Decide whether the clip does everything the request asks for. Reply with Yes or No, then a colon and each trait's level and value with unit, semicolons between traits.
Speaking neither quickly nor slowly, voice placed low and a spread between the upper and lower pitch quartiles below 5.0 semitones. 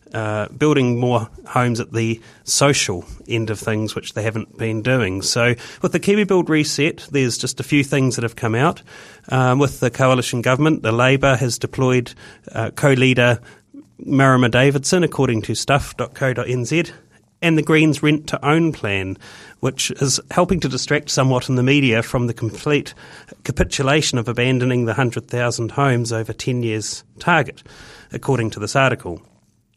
Yes: average, 160 wpm; low, 130 Hz; average, 3.7 semitones